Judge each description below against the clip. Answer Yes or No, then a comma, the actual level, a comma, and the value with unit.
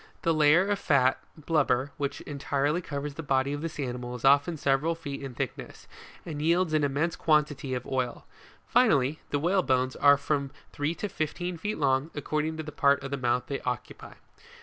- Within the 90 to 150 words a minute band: No, average, 185 wpm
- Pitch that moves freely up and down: No, average, 2.7 semitones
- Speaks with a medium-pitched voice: Yes, medium, 145 Hz